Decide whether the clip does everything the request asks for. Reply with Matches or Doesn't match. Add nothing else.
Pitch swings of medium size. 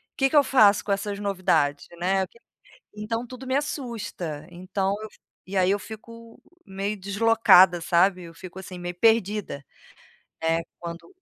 Matches